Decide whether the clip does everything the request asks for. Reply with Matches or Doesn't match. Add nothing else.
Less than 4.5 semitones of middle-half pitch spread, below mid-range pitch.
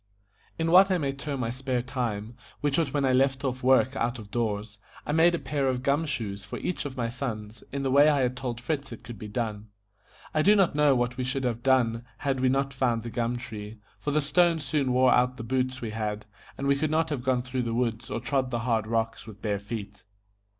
Matches